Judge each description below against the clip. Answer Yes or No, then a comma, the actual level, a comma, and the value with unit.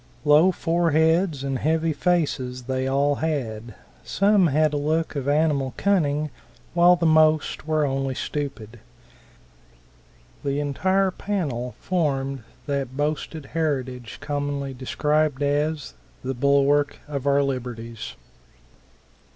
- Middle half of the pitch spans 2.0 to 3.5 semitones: Yes, average, 2.8 semitones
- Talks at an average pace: No, slow, 110 wpm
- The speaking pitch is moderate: Yes, medium, 145 Hz